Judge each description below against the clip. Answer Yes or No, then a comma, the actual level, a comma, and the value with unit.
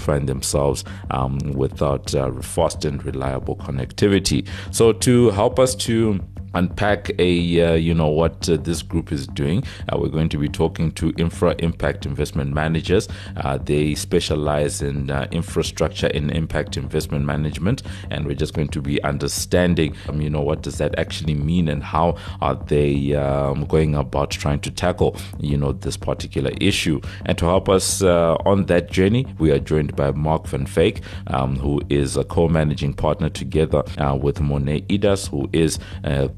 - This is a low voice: Yes, very low, 80 Hz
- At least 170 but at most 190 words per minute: Yes, average, 175 wpm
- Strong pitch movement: No, average, 3.9 semitones